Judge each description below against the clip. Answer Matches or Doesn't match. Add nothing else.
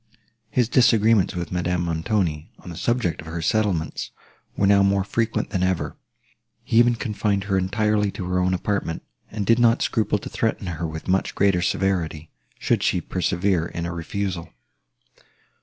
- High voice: Doesn't match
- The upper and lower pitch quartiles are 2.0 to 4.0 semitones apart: Matches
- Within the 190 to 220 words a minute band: Doesn't match